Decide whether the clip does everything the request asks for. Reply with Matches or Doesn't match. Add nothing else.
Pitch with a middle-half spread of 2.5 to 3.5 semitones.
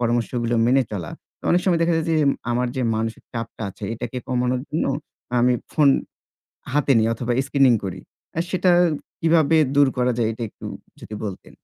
Doesn't match